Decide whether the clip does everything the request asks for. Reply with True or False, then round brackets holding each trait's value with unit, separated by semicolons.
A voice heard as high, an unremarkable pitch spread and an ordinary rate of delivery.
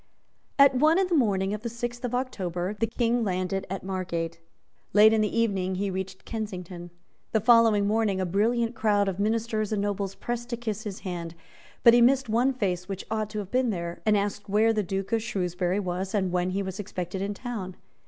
False (205 Hz; 3.4 semitones; 210 wpm)